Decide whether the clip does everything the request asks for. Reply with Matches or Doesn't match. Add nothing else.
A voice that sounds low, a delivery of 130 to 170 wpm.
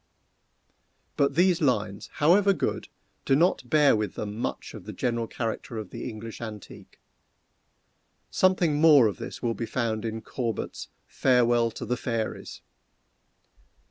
Matches